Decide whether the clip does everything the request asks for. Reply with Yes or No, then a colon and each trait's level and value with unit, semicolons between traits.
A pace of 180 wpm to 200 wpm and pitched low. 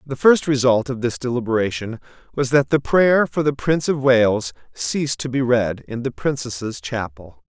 Yes: average, 185 wpm; low, 125 Hz